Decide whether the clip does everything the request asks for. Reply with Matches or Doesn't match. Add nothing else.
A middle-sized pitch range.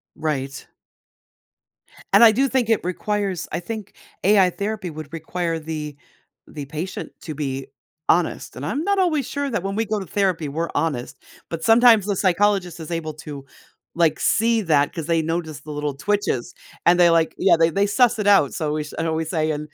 Matches